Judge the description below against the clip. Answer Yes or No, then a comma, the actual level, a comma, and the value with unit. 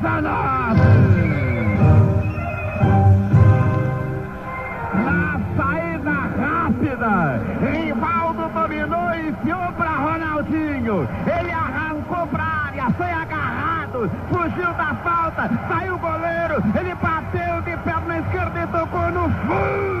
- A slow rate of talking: Yes, slow, 95 wpm